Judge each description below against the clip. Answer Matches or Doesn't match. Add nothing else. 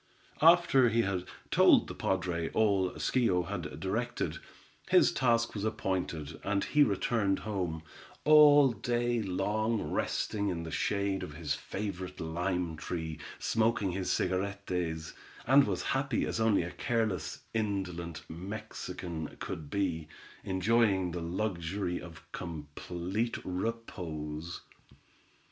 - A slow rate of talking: Matches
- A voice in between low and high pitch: Doesn't match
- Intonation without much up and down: Doesn't match